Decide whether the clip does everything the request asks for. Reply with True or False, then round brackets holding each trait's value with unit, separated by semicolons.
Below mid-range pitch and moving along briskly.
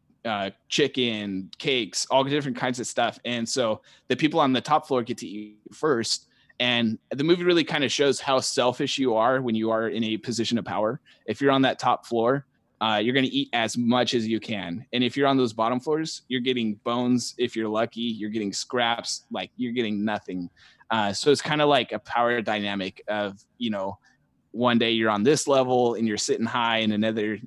True (120 Hz; 215 wpm)